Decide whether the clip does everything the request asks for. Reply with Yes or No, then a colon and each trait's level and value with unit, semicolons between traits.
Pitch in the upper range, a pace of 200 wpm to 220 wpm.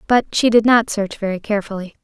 Yes: high, 215 Hz; fast, 205 wpm